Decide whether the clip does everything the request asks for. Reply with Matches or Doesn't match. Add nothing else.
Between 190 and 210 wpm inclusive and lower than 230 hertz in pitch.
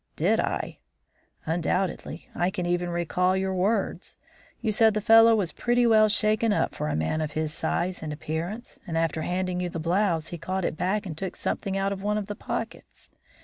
Matches